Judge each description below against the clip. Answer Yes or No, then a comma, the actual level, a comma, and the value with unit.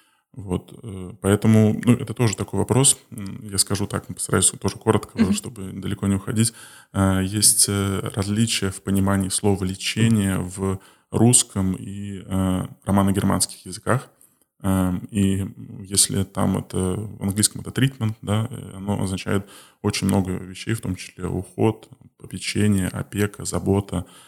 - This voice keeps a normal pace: Yes, average, 120 wpm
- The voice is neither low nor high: No, low, 100 Hz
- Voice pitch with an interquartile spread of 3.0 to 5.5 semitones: No, narrow, 2.4 semitones